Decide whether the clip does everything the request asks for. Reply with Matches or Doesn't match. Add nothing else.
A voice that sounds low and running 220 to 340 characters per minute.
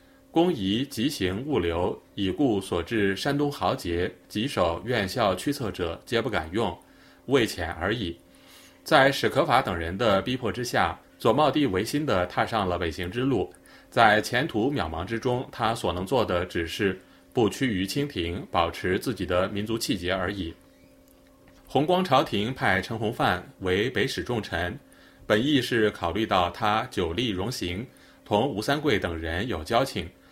Matches